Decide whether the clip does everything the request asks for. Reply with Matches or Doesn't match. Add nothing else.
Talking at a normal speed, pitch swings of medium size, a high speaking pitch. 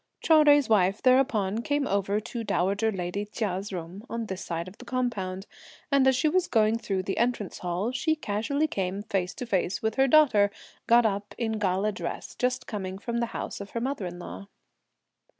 Matches